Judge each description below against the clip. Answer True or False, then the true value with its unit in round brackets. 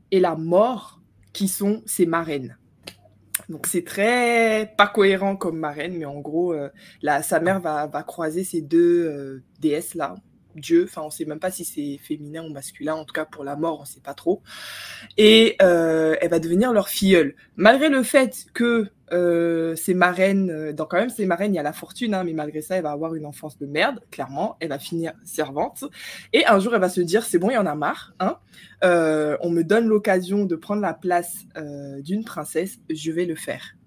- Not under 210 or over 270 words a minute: True (215 wpm)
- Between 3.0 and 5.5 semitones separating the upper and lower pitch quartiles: True (4.0 semitones)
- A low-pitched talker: False (170 Hz)